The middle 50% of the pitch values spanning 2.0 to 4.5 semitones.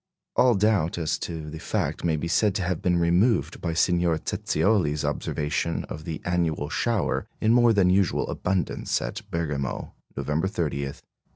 Yes: average, 3.7 semitones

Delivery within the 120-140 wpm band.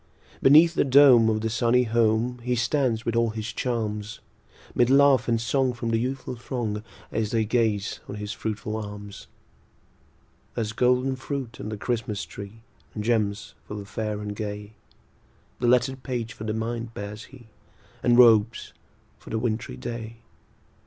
No: average, 160 wpm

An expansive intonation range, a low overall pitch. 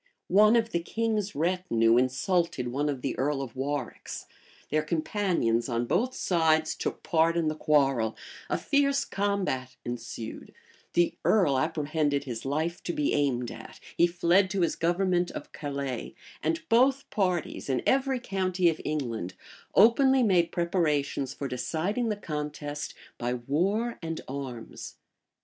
No: wide, 6.0 semitones; medium, 160 Hz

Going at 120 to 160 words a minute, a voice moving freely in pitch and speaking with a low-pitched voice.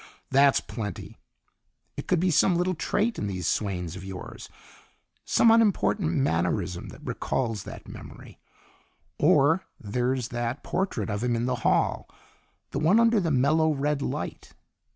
Yes: average, 145 wpm; wide, 8.5 semitones; low, 130 Hz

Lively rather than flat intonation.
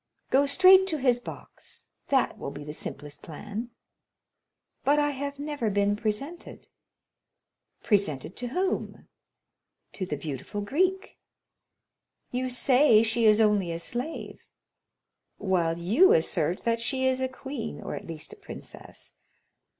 Yes: wide, 7.0 semitones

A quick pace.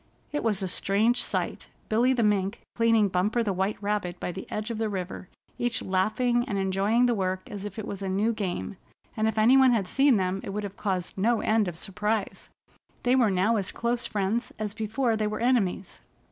Yes: fast, 215 wpm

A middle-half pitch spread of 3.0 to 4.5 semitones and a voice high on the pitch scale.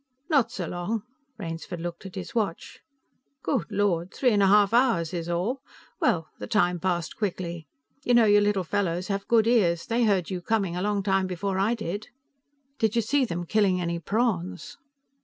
Yes: average, 4.0 semitones; high, 195 Hz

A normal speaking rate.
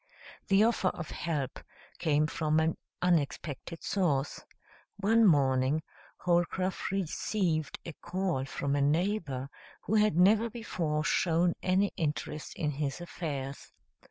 No: slow, 120 wpm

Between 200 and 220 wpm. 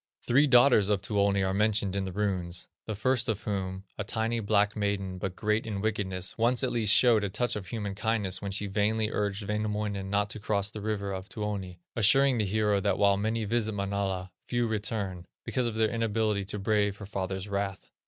Yes: fast, 205 wpm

